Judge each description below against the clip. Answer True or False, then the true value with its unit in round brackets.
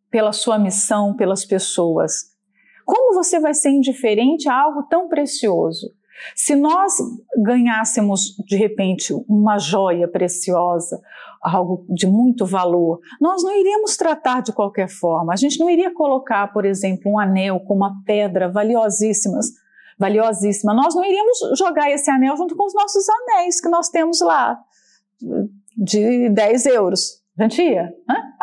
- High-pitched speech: True (220 Hz)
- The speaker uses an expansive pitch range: True (7.3 semitones)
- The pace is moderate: True (140 wpm)